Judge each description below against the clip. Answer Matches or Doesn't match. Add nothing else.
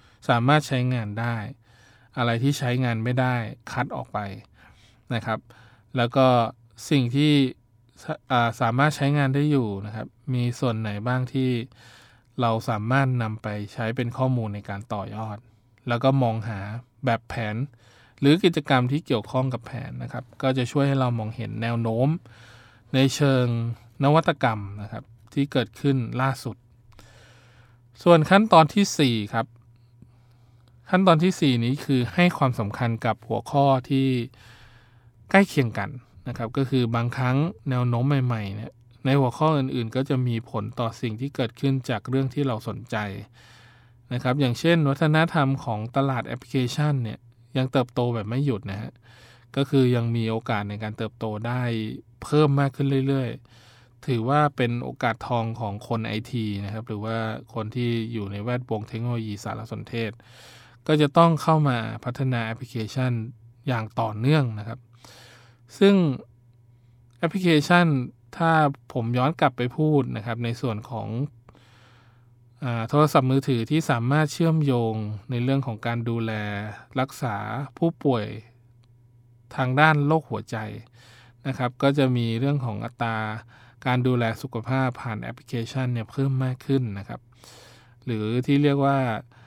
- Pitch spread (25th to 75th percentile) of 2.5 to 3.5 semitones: Matches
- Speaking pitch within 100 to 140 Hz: Matches